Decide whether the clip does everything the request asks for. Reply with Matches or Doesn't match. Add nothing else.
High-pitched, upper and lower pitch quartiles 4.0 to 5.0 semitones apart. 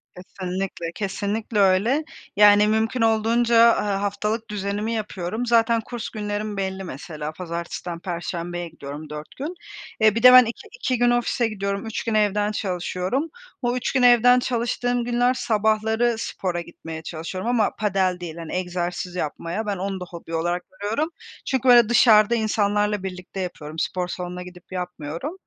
Matches